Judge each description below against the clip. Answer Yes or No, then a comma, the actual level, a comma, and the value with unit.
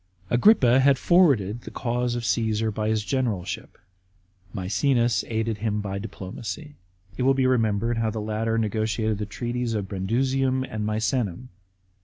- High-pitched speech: No, low, 115 Hz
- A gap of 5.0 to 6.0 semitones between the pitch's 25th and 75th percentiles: No, average, 2.8 semitones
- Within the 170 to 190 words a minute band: No, average, 150 wpm